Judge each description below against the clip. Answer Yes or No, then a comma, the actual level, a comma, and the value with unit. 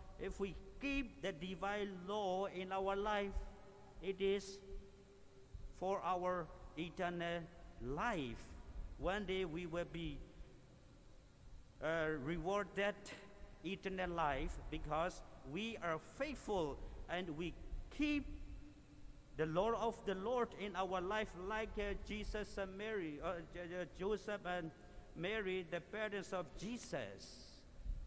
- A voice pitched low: No, medium, 185 Hz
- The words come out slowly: Yes, slow, 115 wpm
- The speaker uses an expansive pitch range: No, average, 4.2 semitones